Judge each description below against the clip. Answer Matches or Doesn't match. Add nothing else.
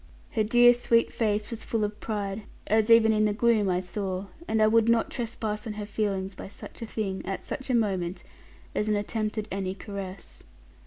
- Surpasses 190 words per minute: Matches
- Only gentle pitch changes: Matches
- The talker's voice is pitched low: Doesn't match